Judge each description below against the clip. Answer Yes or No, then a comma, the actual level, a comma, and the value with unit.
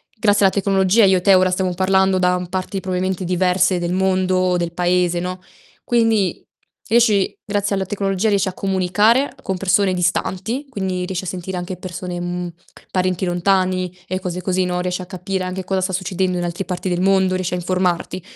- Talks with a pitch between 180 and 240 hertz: Yes, medium, 185 Hz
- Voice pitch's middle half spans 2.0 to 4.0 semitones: No, narrow, 1.2 semitones